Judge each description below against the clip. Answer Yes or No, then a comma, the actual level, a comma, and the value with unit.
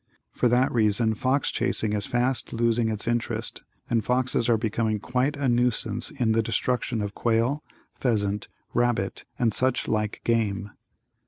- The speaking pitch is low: Yes, low, 115 Hz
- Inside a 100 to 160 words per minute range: Yes, average, 150 wpm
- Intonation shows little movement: Yes, narrow, 2.3 semitones